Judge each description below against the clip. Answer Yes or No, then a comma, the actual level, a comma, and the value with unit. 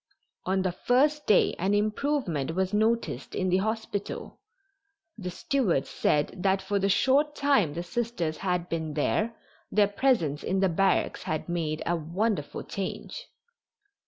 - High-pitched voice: Yes, high, 195 Hz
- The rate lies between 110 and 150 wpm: Yes, average, 145 wpm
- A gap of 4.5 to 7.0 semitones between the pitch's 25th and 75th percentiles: Yes, average, 4.8 semitones